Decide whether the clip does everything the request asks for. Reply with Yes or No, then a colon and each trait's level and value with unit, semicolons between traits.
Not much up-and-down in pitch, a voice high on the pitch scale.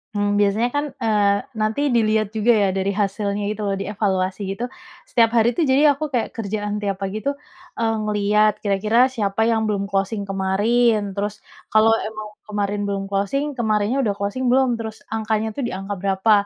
Yes: narrow, 2.2 semitones; high, 210 Hz